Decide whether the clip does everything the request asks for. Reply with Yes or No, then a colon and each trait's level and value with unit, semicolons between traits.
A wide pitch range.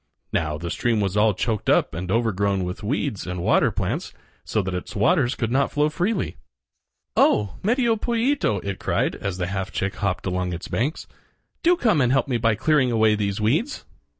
Yes: wide, 7.1 semitones